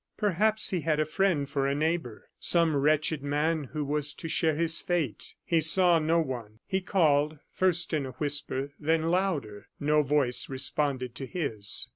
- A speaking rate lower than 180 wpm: Yes, average, 170 wpm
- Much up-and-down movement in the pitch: No, average, 3.0 semitones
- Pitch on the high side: No, medium, 150 Hz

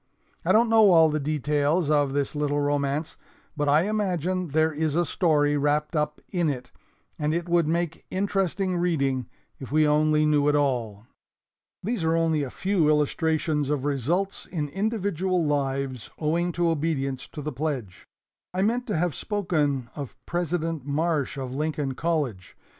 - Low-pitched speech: No, medium, 155 Hz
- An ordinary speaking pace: Yes, average, 160 wpm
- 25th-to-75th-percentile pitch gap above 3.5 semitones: No, average, 3.2 semitones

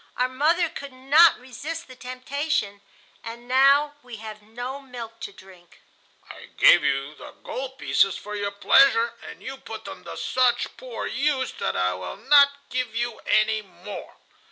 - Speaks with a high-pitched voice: Yes, very high, 250 Hz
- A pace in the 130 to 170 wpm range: Yes, average, 165 wpm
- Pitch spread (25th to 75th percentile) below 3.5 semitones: No, average, 4.4 semitones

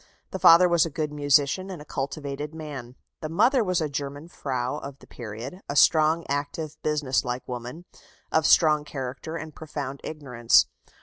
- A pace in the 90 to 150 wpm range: No, average, 170 wpm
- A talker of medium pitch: Yes, medium, 150 Hz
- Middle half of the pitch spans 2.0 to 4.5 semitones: Yes, average, 2.8 semitones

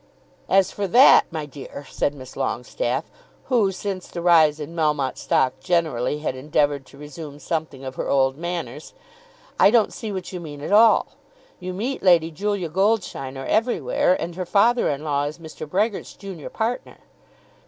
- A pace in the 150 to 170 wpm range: Yes, average, 165 wpm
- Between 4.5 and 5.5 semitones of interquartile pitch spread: Yes, average, 5.1 semitones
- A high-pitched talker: No, medium, 165 Hz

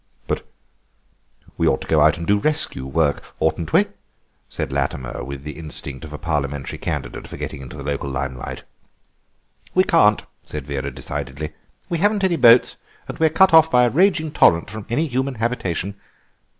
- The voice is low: Yes, very low, 85 Hz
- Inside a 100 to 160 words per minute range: No, average, 175 wpm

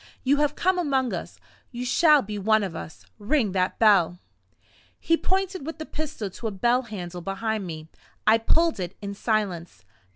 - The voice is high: Yes, high, 220 Hz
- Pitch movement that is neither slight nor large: No, wide, 7.0 semitones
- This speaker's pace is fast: No, average, 175 wpm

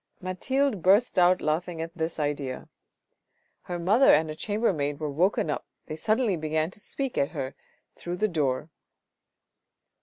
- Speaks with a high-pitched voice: No, medium, 170 Hz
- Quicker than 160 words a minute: No, average, 155 wpm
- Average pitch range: Yes, average, 4.7 semitones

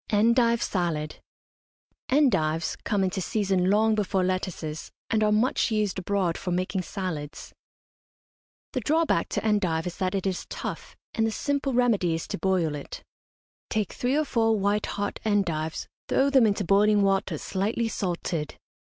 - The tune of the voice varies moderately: Yes, average, 3.7 semitones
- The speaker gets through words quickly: No, average, 155 wpm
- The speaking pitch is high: Yes, high, 200 Hz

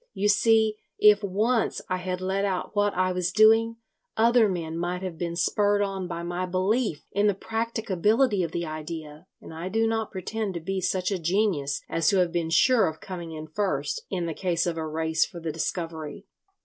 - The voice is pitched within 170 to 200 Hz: Yes, medium, 185 Hz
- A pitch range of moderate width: Yes, average, 3.7 semitones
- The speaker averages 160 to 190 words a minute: No, average, 200 wpm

